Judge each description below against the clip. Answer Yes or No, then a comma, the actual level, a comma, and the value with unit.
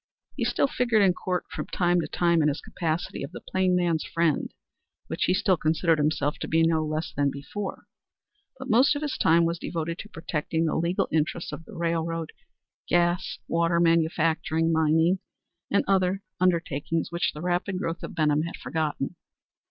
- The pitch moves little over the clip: Yes, narrow, 2.1 semitones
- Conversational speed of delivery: Yes, average, 175 wpm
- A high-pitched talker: No, medium, 165 Hz